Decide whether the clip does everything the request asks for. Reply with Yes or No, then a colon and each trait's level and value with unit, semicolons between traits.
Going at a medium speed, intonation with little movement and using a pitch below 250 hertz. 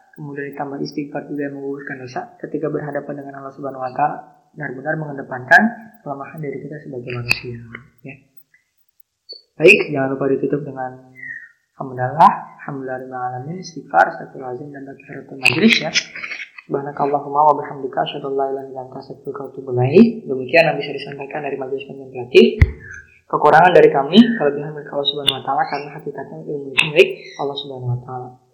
No: fast, 160 wpm; narrow, 1.7 semitones; medium, 140 Hz